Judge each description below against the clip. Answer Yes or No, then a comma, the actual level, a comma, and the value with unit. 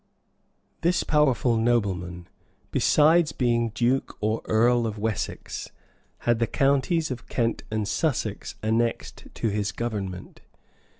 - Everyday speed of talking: No, slow, 120 wpm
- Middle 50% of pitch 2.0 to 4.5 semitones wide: Yes, average, 3.5 semitones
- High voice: No, low, 115 Hz